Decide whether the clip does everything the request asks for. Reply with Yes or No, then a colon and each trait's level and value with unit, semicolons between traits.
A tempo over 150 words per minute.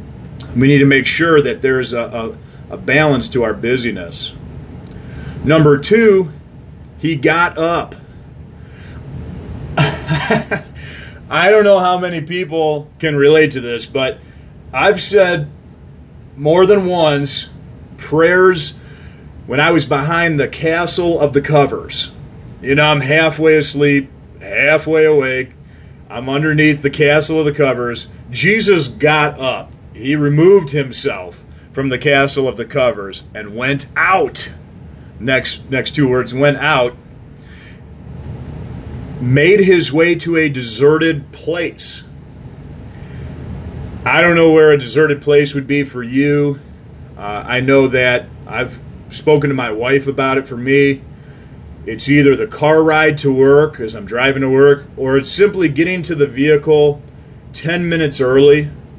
No: slow, 135 wpm